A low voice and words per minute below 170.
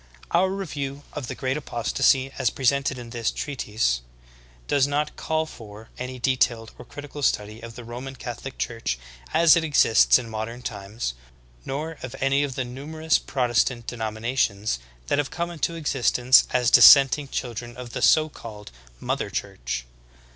Yes: low, 125 Hz; average, 160 wpm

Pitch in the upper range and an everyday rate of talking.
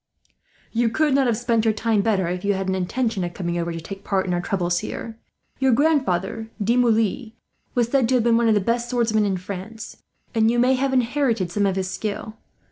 No: high, 220 Hz; fast, 220 wpm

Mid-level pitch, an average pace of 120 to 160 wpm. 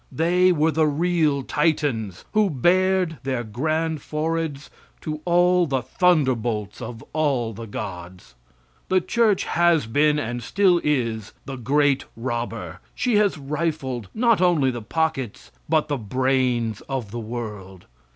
Yes: medium, 145 Hz; slow, 135 wpm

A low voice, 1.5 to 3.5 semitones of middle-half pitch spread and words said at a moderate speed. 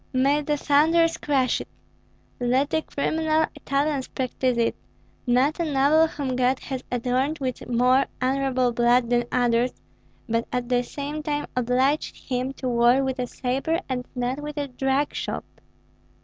No: very high, 265 Hz; average, 2.7 semitones; average, 155 wpm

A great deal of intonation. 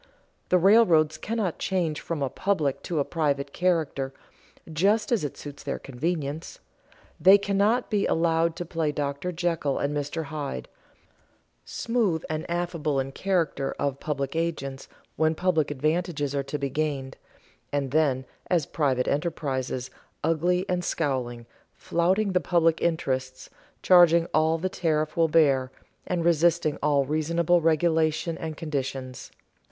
No: average, 3.4 semitones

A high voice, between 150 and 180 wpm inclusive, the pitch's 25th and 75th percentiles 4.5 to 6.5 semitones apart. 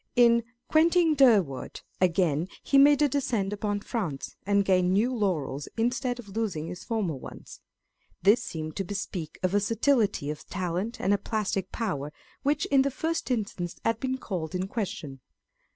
Yes: high, 205 Hz; average, 160 wpm; wide, 5.4 semitones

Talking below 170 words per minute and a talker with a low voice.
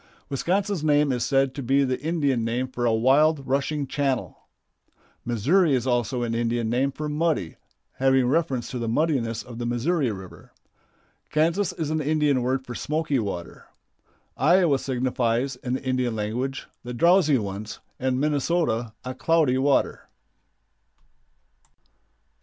Yes: average, 140 wpm; low, 130 Hz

